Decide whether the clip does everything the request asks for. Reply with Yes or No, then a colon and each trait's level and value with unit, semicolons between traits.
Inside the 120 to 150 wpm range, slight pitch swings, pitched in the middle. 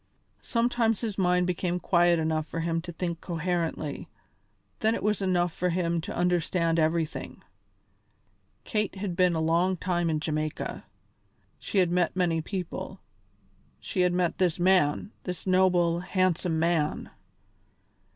Yes: average, 140 wpm; narrow, 1.9 semitones; medium, 175 Hz